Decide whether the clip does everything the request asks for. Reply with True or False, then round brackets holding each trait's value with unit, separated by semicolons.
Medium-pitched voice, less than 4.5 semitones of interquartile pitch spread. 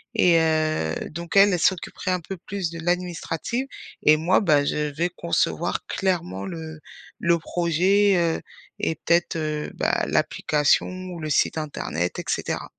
True (170 Hz; 2.7 semitones)